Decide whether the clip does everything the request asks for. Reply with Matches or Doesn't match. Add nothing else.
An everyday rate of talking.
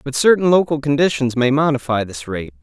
Matches